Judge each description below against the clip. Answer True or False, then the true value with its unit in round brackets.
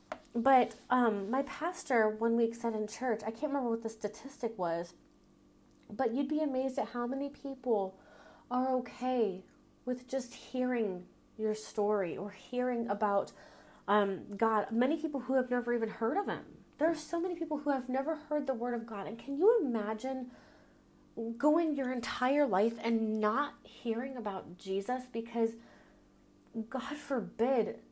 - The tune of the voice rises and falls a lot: False (3.5 semitones)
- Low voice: False (245 Hz)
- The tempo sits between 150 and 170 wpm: True (160 wpm)